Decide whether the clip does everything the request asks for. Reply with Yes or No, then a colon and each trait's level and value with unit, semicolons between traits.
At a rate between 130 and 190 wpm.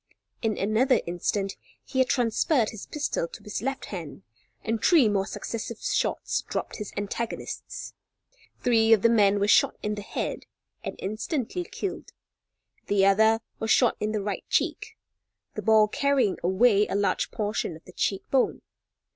Yes: average, 160 wpm